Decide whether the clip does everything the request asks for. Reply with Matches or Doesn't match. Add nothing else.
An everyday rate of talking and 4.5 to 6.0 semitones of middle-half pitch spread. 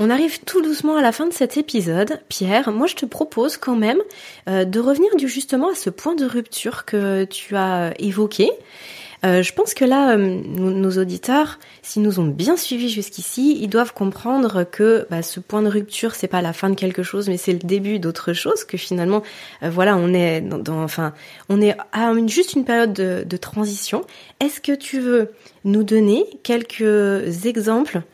Matches